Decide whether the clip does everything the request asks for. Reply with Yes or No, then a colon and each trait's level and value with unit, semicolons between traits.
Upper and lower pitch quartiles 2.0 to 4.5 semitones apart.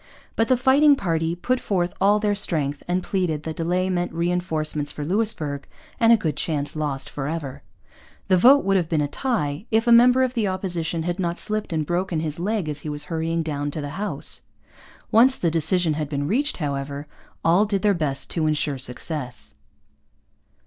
No: average, 5.3 semitones